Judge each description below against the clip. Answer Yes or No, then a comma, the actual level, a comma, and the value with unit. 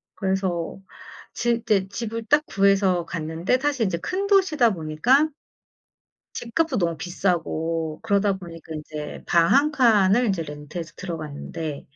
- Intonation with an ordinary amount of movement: No, wide, 6.0 semitones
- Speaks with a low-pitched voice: No, high, 190 Hz